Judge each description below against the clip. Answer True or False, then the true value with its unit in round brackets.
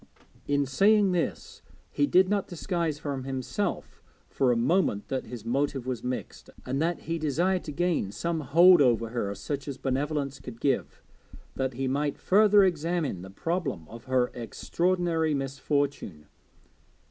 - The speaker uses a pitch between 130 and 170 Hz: True (140 Hz)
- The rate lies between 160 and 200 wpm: False (150 wpm)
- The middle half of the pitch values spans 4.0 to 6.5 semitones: True (5.1 semitones)